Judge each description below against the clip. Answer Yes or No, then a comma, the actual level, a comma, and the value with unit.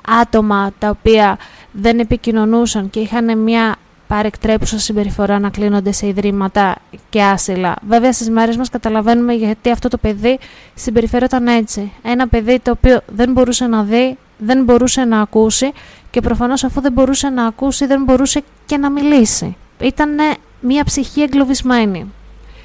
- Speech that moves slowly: No, average, 145 wpm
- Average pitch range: Yes, average, 3.3 semitones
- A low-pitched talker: No, high, 235 Hz